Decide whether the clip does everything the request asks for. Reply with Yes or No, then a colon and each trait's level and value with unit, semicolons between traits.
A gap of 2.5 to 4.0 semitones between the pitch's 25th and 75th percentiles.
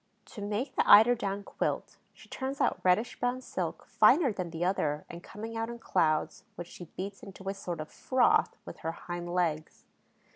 No: average, 4.8 semitones